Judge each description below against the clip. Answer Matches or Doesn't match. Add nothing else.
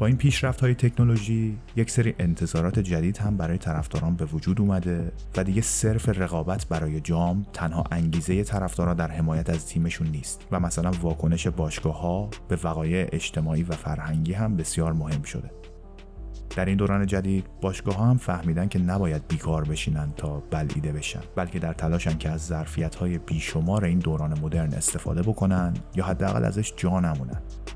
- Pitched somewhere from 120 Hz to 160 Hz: Doesn't match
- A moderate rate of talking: Doesn't match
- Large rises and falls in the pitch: Doesn't match